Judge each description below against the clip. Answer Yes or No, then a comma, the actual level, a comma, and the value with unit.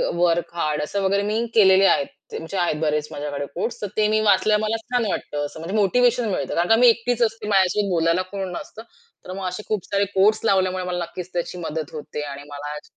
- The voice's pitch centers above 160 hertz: Yes, medium, 185 Hz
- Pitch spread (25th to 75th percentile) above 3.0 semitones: Yes, average, 4.1 semitones